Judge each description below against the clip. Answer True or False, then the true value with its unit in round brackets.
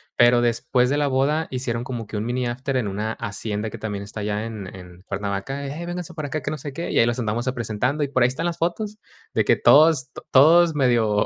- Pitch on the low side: True (125 Hz)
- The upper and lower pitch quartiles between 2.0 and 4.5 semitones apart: False (5.0 semitones)